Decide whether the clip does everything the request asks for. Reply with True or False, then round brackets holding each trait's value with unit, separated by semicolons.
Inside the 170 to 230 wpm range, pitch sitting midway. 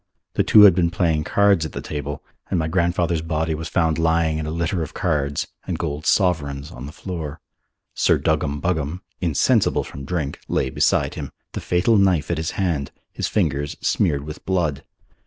False (185 wpm; 80 Hz)